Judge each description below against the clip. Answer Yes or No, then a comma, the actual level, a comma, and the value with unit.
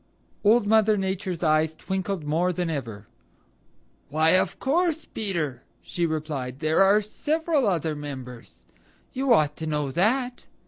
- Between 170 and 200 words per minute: No, slow, 135 wpm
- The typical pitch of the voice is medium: Yes, medium, 175 Hz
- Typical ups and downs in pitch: No, wide, 5.8 semitones